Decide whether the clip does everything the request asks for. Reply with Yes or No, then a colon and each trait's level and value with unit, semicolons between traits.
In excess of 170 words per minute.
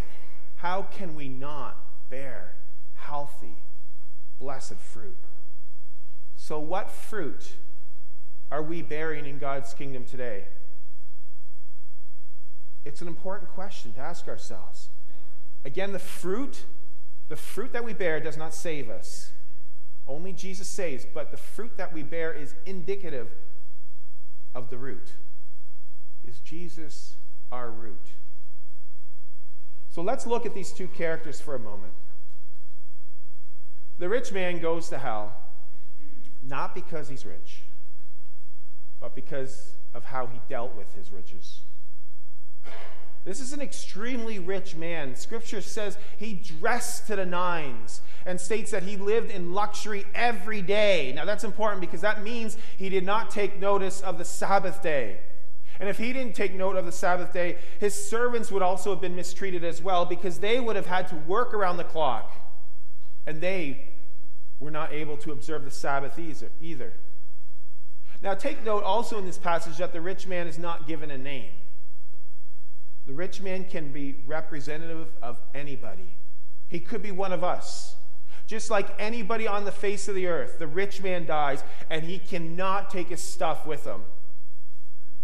No: average, 150 wpm